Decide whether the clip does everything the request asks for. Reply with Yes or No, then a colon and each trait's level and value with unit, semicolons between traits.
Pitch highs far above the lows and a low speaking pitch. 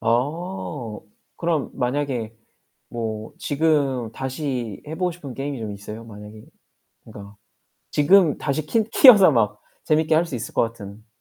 Yes: wide, 6.0 semitones; low, 130 Hz